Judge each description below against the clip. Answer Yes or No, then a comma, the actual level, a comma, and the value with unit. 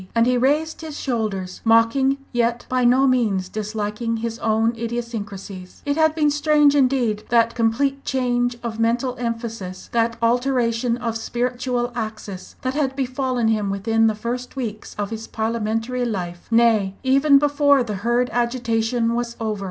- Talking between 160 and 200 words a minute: No, average, 150 wpm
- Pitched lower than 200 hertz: No, high, 235 Hz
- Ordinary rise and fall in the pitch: No, narrow, 2.3 semitones